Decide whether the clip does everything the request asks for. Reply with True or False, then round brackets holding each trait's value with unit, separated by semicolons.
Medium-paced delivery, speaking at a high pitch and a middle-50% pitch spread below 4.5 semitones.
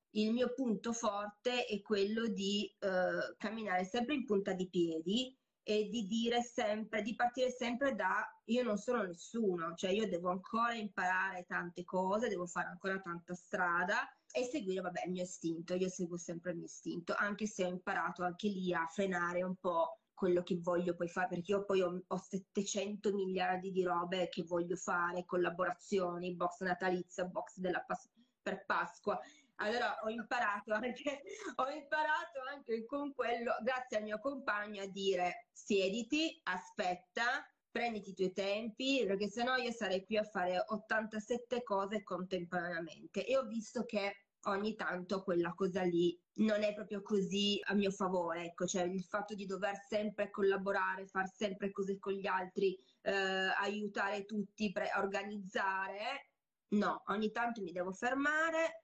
True (160 wpm; 200 Hz; 3.4 semitones)